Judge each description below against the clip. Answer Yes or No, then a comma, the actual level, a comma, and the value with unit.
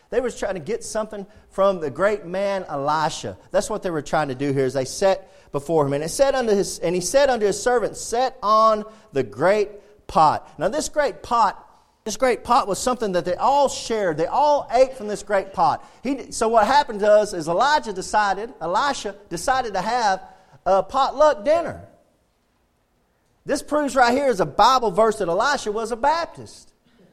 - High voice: Yes, high, 210 Hz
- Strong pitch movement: Yes, wide, 5.8 semitones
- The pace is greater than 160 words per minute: Yes, average, 190 wpm